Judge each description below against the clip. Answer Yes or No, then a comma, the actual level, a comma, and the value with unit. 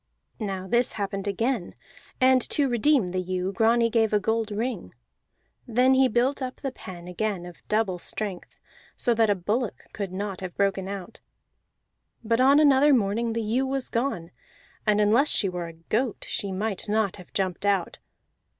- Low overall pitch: No, high, 215 Hz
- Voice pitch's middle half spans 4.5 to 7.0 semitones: No, average, 4.1 semitones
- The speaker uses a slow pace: No, average, 170 wpm